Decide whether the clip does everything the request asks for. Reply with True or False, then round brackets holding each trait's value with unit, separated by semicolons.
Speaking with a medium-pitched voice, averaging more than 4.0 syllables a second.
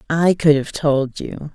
False (150 Hz; 3.7 syllables/s)